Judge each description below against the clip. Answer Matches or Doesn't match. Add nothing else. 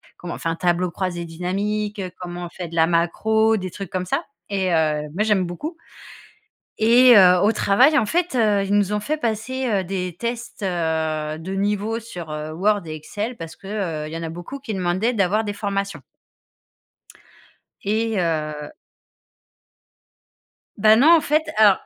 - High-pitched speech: Matches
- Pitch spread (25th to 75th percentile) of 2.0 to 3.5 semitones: Doesn't match